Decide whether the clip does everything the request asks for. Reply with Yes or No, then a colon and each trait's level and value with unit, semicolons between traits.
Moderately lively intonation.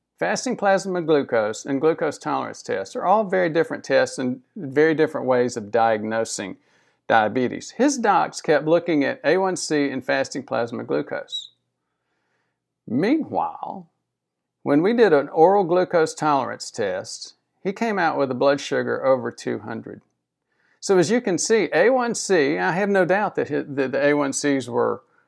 No: wide, 6.7 semitones